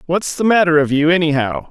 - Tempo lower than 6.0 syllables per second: Yes, 5.7 syllables/s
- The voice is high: No, medium, 160 Hz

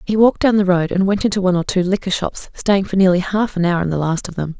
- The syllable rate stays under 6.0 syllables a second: No, 6.5 syllables/s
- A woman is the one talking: Yes, female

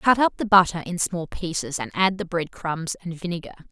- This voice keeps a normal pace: No, fast, 225 wpm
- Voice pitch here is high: No, medium, 175 Hz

